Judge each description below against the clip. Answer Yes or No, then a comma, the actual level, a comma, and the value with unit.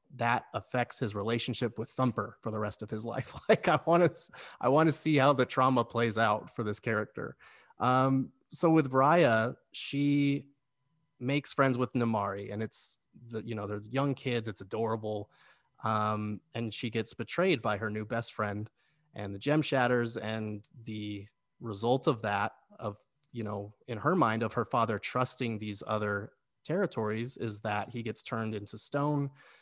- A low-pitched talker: Yes, low, 115 Hz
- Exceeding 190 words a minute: No, average, 170 wpm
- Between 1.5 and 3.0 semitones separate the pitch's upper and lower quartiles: No, average, 3.7 semitones